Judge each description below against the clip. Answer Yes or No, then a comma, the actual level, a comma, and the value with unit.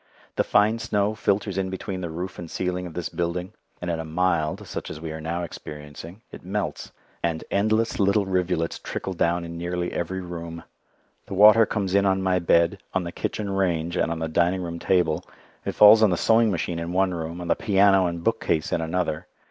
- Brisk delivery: Yes, fast, 210 wpm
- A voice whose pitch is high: No, very low, 90 Hz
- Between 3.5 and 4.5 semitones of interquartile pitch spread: No, narrow, 2.6 semitones